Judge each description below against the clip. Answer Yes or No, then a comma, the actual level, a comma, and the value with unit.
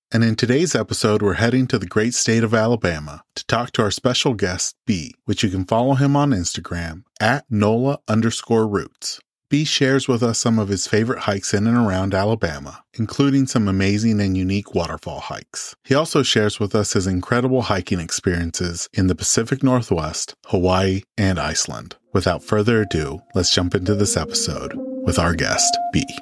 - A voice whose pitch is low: Yes, low, 110 Hz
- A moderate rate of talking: Yes, average, 180 wpm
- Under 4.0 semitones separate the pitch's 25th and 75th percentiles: No, average, 4.6 semitones